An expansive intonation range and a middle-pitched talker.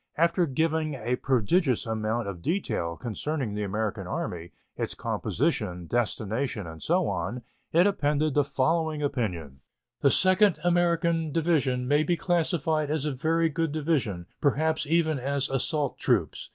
Yes: wide, 5.9 semitones; medium, 145 Hz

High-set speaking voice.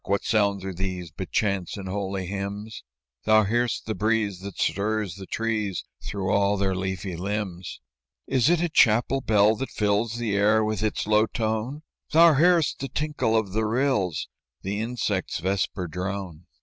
No: low, 105 Hz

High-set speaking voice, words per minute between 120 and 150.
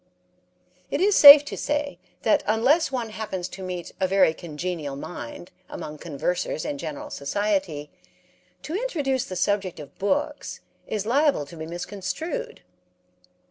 Yes: high, 195 Hz; average, 140 wpm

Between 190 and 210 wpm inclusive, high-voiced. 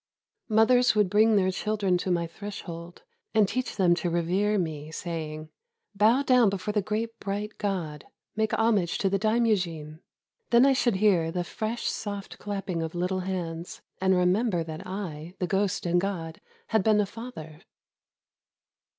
No: average, 160 wpm; high, 195 Hz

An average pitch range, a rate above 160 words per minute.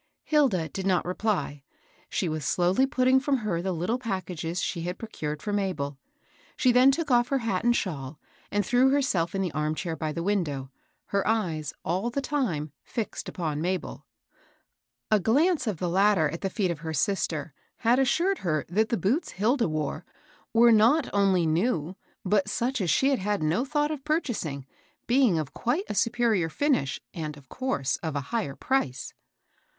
No: wide, 7.1 semitones; average, 180 wpm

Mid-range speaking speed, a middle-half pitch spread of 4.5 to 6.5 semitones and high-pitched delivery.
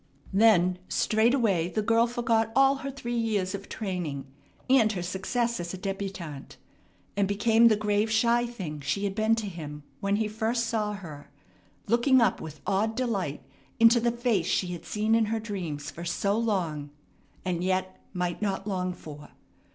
No: average, 170 wpm; average, 4.1 semitones; high, 205 Hz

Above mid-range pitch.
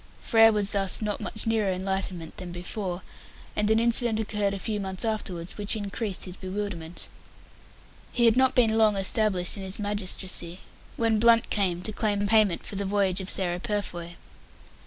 Yes: high, 205 Hz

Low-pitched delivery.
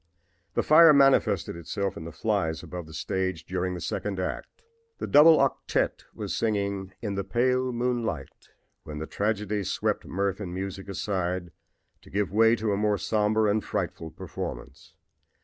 Yes: low, 100 Hz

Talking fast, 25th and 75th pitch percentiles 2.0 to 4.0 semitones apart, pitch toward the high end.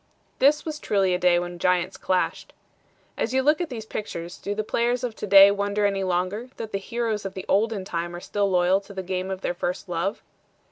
Yes: fast, 225 wpm; average, 3.3 semitones; high, 195 Hz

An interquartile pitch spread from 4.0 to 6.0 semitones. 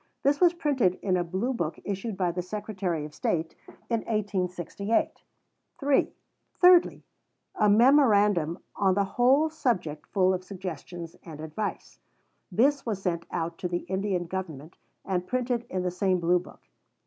Yes: average, 4.7 semitones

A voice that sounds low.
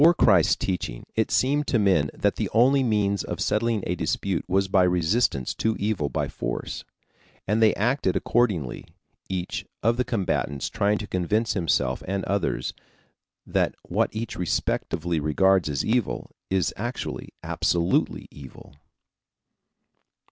Yes: low, 100 Hz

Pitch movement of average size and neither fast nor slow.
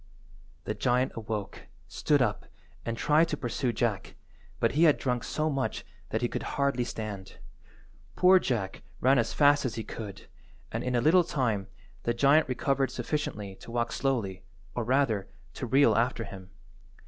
Yes: average, 4.1 semitones; average, 165 wpm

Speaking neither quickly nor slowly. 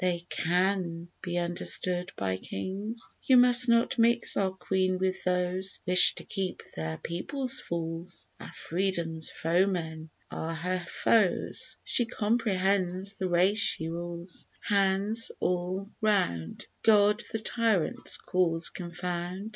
No: slow, 125 wpm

